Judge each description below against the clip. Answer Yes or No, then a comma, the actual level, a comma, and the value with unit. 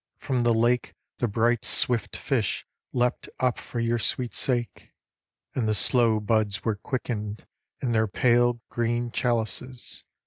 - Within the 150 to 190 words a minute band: No, average, 140 wpm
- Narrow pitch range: Yes, narrow, 1.7 semitones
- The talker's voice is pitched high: No, low, 120 Hz